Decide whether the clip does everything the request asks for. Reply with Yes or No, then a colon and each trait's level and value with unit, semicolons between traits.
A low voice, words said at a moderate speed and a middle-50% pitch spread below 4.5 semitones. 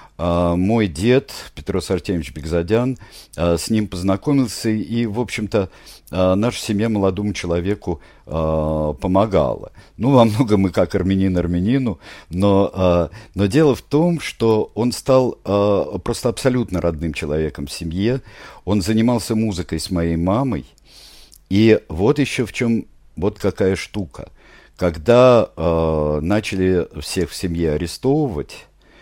No: low, 100 Hz; average, 130 wpm; average, 4.8 semitones